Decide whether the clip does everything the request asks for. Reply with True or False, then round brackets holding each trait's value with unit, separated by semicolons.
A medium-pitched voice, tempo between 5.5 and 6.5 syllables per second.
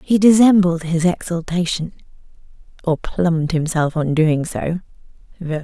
False (170 Hz; 4.4 syllables/s)